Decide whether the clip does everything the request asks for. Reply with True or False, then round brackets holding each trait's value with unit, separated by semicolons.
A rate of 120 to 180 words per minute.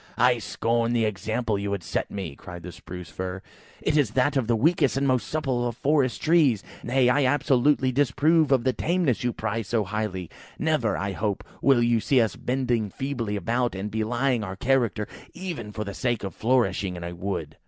False (195 wpm)